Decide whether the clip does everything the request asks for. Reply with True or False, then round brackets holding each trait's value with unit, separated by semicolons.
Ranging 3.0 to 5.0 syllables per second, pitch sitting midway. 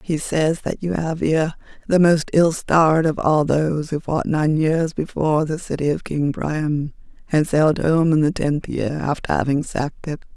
True (4.7 syllables/s; 155 Hz)